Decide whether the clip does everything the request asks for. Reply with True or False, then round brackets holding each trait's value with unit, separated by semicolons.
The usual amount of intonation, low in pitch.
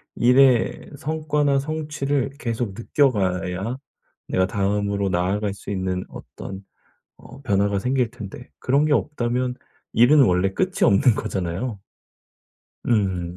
False (5.8 semitones; 115 Hz)